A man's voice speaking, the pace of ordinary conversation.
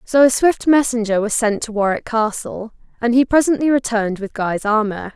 No: female; average, 185 wpm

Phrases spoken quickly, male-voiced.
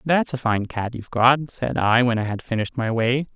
Yes: fast, 250 wpm; male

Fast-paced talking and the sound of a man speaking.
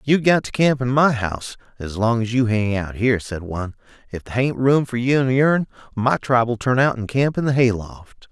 Yes: fast, 245 wpm; male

